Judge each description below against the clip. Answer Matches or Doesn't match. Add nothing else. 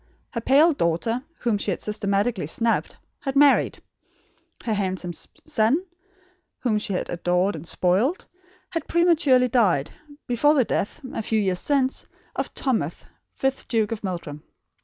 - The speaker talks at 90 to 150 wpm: Matches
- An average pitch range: Doesn't match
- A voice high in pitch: Matches